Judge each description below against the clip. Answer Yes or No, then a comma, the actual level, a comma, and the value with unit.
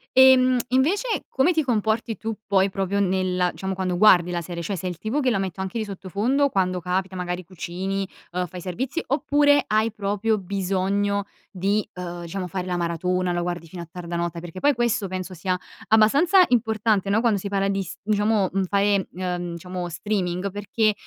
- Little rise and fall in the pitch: No, average, 3.3 semitones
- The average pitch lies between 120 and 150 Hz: No, high, 195 Hz